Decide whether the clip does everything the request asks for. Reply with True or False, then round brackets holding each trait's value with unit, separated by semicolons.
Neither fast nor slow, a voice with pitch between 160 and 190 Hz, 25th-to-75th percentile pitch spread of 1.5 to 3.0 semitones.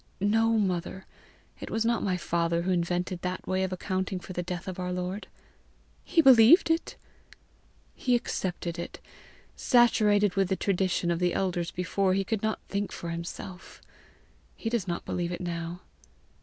True (160 wpm; 185 Hz; 2.7 semitones)